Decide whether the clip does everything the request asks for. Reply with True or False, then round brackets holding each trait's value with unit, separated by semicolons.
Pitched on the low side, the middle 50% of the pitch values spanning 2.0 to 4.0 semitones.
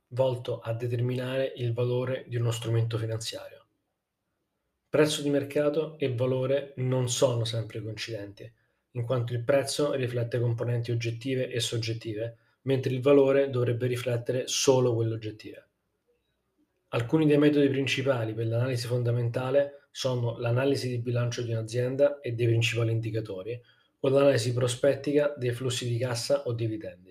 True (125 Hz; 2.6 semitones)